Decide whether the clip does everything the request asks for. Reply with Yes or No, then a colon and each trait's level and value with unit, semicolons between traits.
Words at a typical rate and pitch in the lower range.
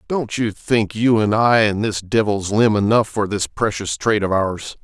No: fast, 210 wpm; low, 105 Hz